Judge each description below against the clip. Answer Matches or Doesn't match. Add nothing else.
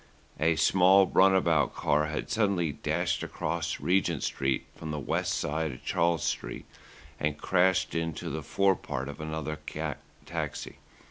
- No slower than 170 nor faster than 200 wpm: Doesn't match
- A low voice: Matches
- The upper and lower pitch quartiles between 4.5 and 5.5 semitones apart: Doesn't match